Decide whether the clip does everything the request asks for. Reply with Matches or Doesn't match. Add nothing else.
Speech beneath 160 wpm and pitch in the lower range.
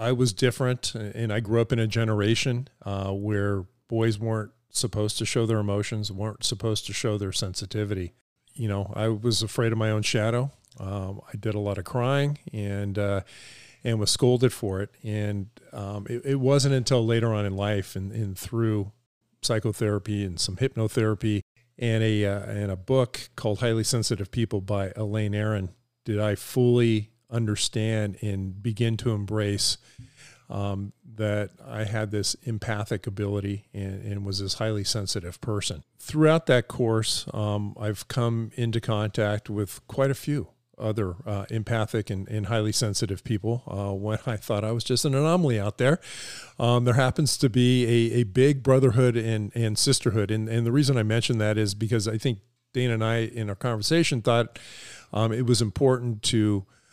Doesn't match